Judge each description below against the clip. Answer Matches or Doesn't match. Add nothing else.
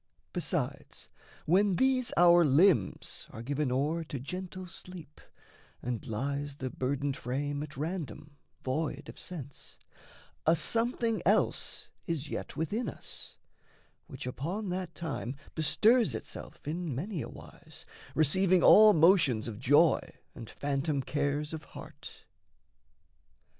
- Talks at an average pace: Doesn't match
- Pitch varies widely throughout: Doesn't match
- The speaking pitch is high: Doesn't match